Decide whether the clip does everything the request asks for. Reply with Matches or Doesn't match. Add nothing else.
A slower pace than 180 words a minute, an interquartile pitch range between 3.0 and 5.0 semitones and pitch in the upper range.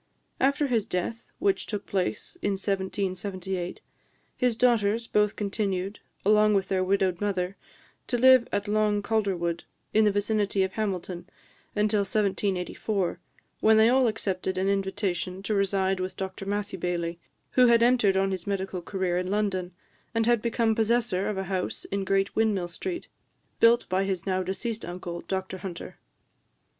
Doesn't match